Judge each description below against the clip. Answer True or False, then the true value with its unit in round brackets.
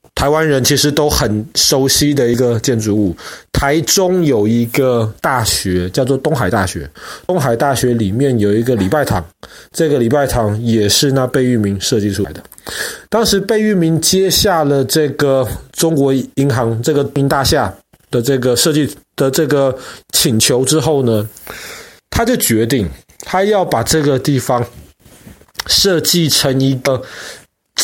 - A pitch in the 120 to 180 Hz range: True (135 Hz)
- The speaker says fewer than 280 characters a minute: True (225 characters per minute)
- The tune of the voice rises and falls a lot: False (4.8 semitones)